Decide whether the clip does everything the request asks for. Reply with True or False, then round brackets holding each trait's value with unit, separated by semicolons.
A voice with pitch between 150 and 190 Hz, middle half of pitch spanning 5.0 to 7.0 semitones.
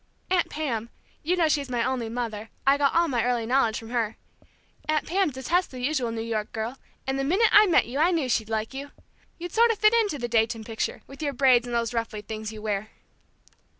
False (250 Hz; 5.4 semitones)